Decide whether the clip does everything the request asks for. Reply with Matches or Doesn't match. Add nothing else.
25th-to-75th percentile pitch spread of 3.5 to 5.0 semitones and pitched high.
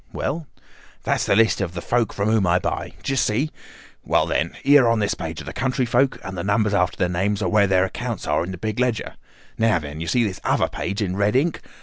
Doesn't match